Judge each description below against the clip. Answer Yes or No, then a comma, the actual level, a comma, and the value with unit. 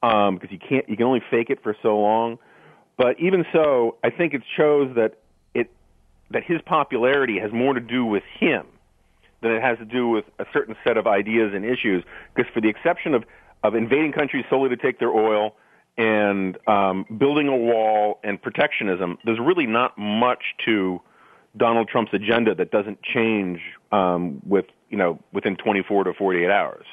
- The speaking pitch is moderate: No, low, 115 Hz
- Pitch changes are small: No, average, 3.3 semitones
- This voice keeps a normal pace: Yes, average, 185 wpm